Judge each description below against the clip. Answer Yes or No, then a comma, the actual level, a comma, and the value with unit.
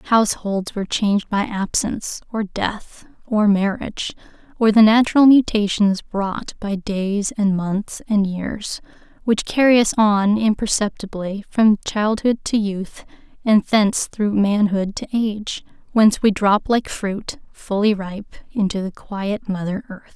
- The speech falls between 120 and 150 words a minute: Yes, average, 140 wpm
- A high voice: Yes, high, 205 Hz